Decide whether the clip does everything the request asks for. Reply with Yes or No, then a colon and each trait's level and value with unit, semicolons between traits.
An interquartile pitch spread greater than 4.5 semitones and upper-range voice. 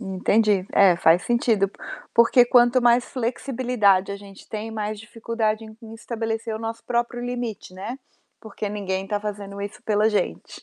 No: average, 2.7 semitones; high, 220 Hz